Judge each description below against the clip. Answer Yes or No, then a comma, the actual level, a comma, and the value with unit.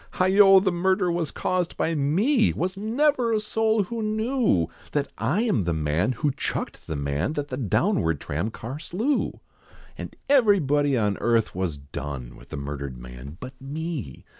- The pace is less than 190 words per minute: Yes, average, 165 wpm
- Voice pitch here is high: No, medium, 145 Hz